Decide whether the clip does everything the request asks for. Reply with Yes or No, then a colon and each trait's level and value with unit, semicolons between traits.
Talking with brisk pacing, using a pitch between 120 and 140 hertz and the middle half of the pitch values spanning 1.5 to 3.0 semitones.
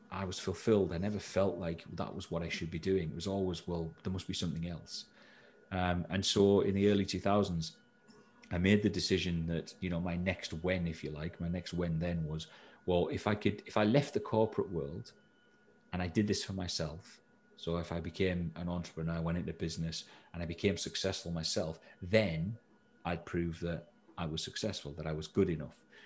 No: fast, 210 wpm; very low, 85 Hz; narrow, 2.4 semitones